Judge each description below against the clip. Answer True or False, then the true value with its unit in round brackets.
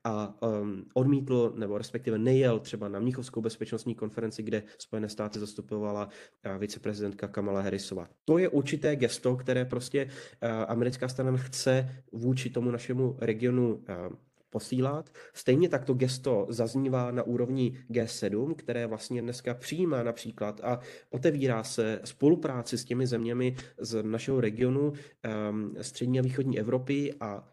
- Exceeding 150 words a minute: False (130 wpm)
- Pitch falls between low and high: False (120 Hz)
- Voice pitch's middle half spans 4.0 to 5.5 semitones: False (2.9 semitones)